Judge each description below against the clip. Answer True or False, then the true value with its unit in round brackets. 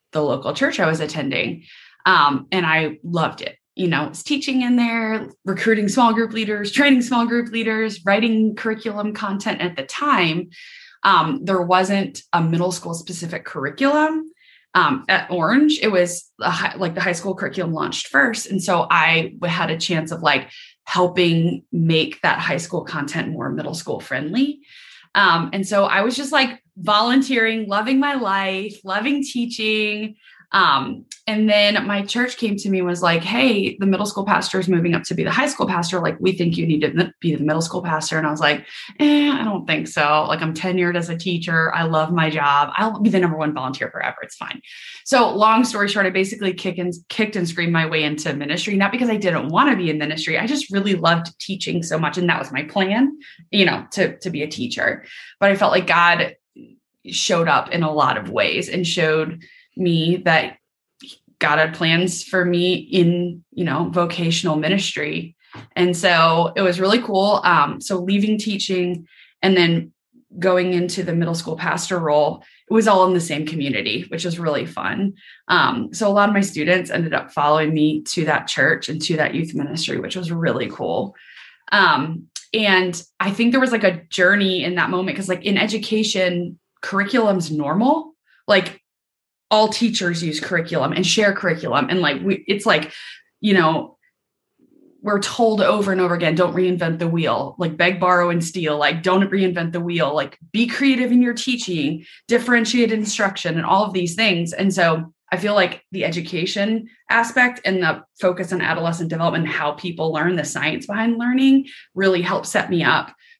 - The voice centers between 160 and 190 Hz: True (185 Hz)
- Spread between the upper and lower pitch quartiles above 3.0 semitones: True (4.2 semitones)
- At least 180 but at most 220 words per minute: True (190 wpm)